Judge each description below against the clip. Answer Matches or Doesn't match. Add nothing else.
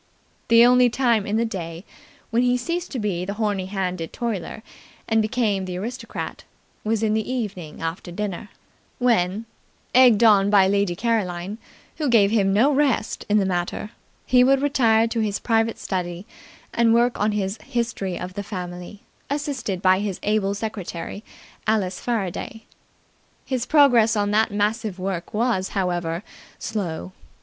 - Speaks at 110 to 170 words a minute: Matches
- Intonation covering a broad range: Doesn't match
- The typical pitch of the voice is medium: Doesn't match